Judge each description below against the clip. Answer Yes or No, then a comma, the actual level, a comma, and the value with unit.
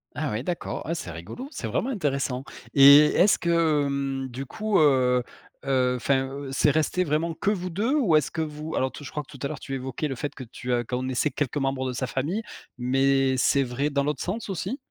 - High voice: No, medium, 140 Hz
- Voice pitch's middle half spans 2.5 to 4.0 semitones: Yes, average, 3.4 semitones